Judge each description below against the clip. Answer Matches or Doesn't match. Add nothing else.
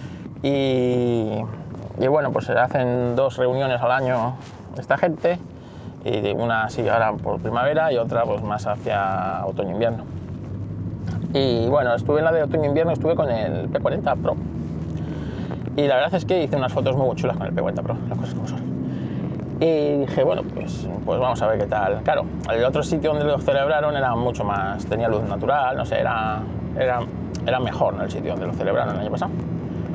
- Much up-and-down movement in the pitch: Matches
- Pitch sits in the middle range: Doesn't match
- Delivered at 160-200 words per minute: Matches